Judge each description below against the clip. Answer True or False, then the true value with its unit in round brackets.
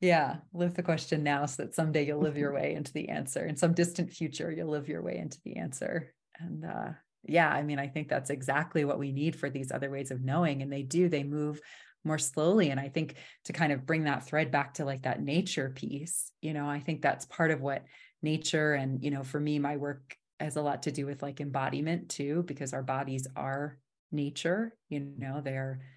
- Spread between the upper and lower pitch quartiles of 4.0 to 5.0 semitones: False (2.4 semitones)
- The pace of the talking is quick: True (230 wpm)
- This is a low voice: False (150 Hz)